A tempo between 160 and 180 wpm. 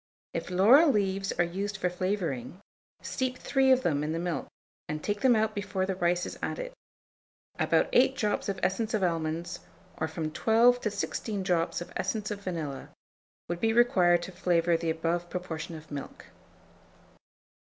Yes: average, 170 wpm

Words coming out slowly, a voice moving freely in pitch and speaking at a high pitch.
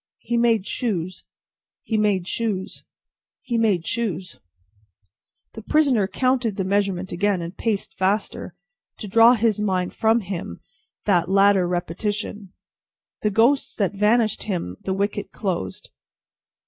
No: slow, 130 wpm; average, 3.2 semitones; high, 205 Hz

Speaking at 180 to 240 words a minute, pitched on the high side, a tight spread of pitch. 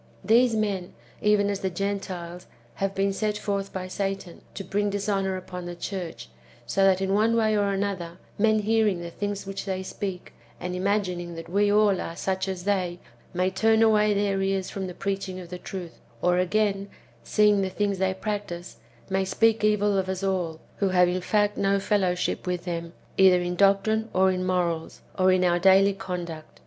Yes: average, 190 wpm; high, 195 Hz; narrow, 2.0 semitones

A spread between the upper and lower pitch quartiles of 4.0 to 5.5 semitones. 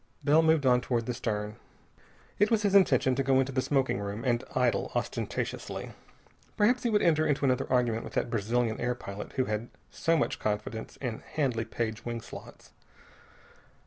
Yes: average, 4.3 semitones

